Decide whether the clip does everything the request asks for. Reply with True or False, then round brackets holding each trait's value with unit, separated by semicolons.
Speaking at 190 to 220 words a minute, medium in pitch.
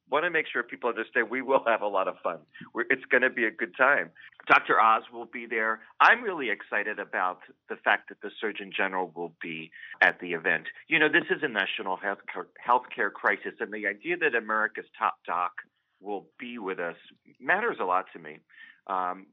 False (205 wpm; 95 Hz)